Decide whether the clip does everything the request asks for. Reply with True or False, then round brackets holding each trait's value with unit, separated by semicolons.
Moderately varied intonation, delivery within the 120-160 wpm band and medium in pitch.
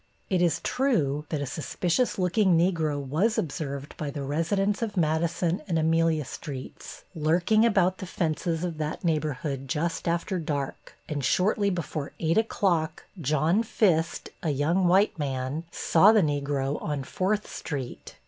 True (4.0 semitones; 150 wpm; 165 Hz)